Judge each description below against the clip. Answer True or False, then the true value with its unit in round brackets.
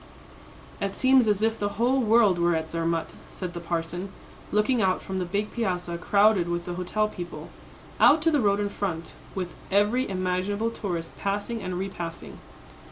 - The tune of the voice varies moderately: True (3.5 semitones)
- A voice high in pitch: True (195 Hz)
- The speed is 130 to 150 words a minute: False (170 wpm)